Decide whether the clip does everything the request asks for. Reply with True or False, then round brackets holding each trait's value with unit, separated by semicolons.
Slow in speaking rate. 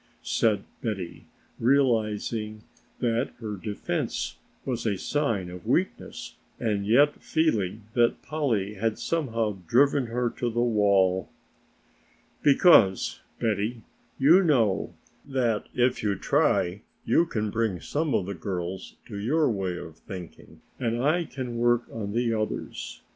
True (130 wpm)